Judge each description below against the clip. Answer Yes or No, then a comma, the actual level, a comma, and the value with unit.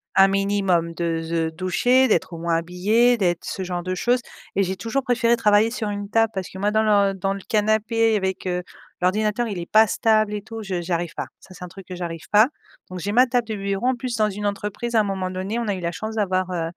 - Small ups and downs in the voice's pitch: No, average, 3.3 semitones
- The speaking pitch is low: No, high, 200 Hz